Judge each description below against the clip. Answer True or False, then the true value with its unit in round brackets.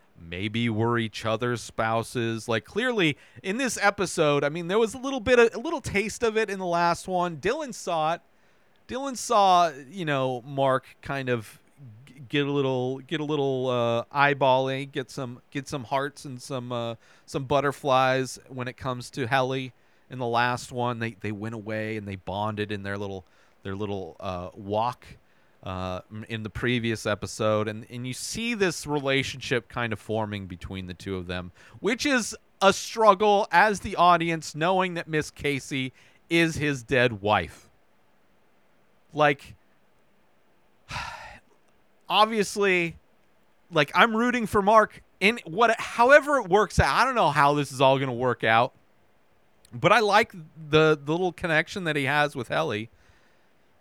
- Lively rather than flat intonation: True (7.5 semitones)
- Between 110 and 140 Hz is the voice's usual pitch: True (135 Hz)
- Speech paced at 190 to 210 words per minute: False (165 wpm)